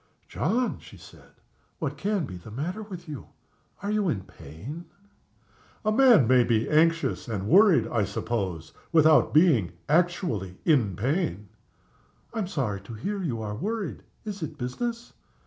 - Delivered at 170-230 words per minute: No, average, 150 wpm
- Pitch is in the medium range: Yes, medium, 150 Hz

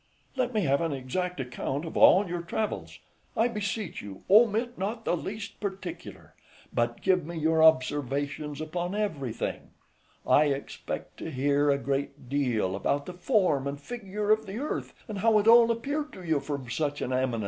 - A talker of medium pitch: Yes, medium, 165 Hz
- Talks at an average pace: Yes, average, 175 wpm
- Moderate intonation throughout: No, wide, 6.9 semitones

